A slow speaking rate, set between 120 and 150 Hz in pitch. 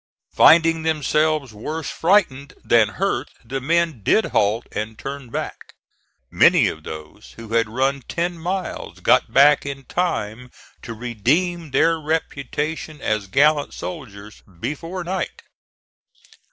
Yes: slow, 125 wpm; medium, 140 Hz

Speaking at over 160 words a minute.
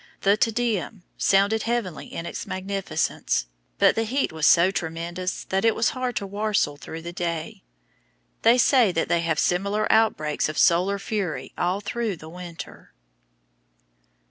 No: average, 155 wpm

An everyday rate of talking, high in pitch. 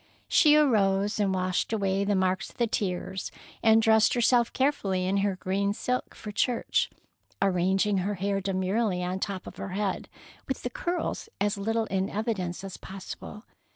Yes: average, 170 wpm; high, 200 Hz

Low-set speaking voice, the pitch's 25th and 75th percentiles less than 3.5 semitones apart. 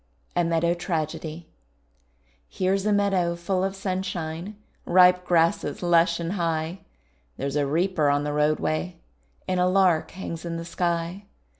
No: medium, 170 Hz; narrow, 2.5 semitones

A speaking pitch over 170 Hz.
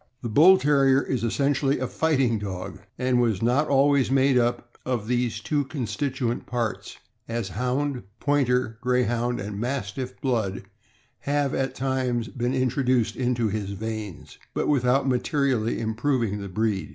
No: low, 125 Hz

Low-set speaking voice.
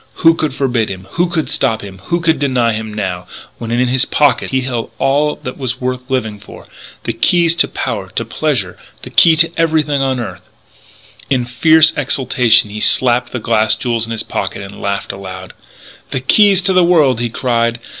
Yes: low, 125 Hz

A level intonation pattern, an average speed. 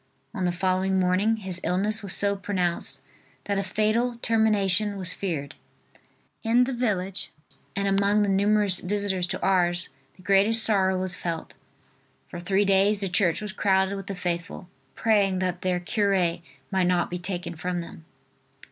Yes: narrow, 2.3 semitones; average, 160 wpm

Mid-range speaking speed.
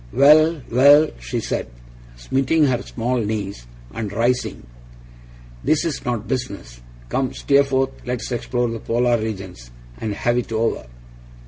No: slow, 130 wpm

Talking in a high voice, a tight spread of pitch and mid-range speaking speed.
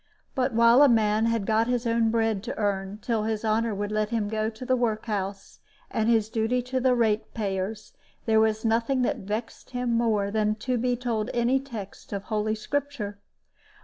Yes: high, 225 Hz; narrow, 2.0 semitones; average, 195 wpm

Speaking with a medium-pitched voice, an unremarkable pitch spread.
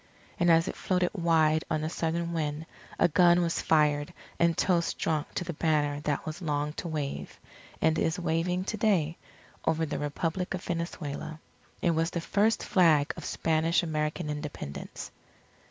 No: medium, 165 Hz; narrow, 2.2 semitones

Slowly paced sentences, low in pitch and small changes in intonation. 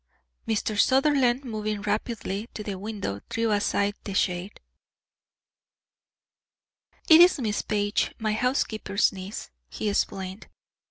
No: slow, 110 wpm; high, 210 Hz; narrow, 2.3 semitones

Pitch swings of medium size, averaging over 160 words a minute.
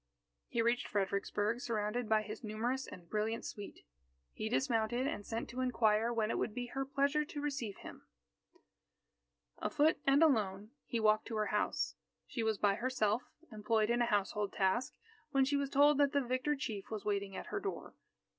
Yes: average, 3.9 semitones; average, 180 wpm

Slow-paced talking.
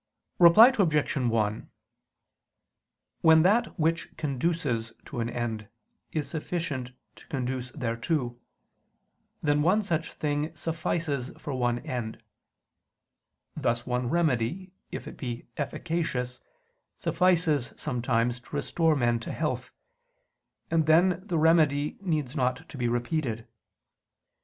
Yes: slow, 115 wpm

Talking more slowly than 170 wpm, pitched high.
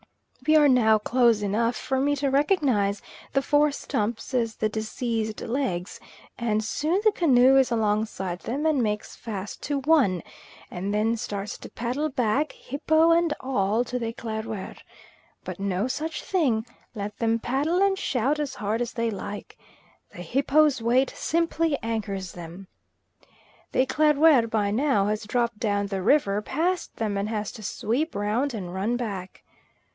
Yes: average, 160 wpm; high, 230 Hz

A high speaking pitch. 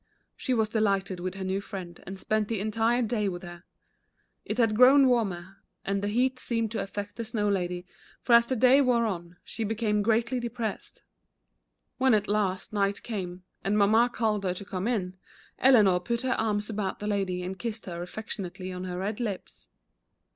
Yes: high, 210 Hz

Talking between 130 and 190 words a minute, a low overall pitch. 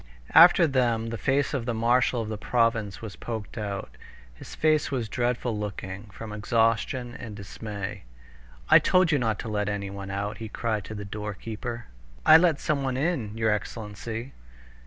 Yes: average, 165 wpm; low, 115 Hz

